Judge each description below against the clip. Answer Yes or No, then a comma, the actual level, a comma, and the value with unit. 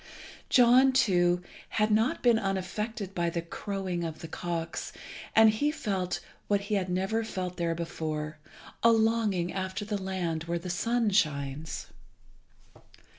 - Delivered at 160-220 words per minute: No, average, 140 wpm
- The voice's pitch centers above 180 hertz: Yes, high, 190 Hz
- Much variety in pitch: No, average, 4.2 semitones